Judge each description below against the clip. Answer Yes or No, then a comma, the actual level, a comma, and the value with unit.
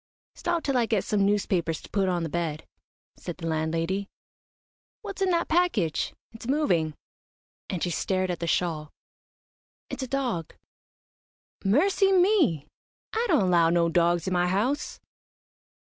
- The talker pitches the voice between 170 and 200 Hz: Yes, high, 190 Hz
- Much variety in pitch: Yes, wide, 8.5 semitones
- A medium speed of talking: Yes, average, 145 wpm